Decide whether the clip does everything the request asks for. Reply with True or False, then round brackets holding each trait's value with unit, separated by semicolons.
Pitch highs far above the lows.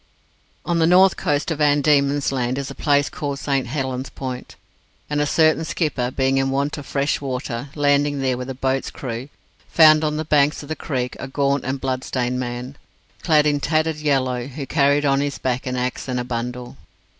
False (2.4 semitones)